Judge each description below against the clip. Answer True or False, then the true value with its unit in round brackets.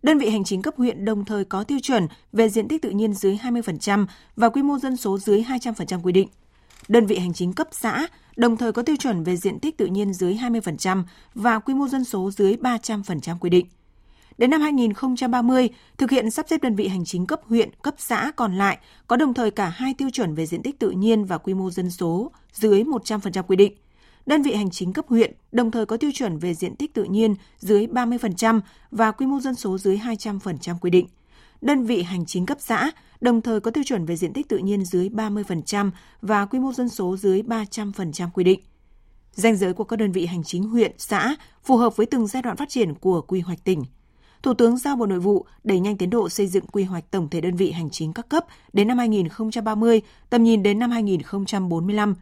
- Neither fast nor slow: True (230 wpm)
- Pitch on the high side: True (215 Hz)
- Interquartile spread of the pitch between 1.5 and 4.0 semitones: False (4.4 semitones)